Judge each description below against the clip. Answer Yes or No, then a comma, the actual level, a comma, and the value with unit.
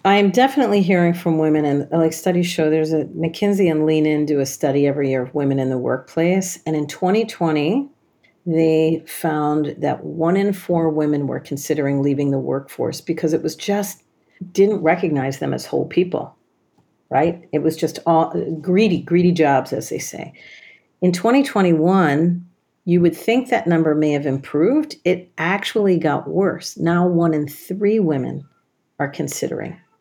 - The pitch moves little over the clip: No, average, 3.3 semitones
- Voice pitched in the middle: Yes, medium, 165 Hz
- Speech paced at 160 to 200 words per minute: Yes, average, 165 wpm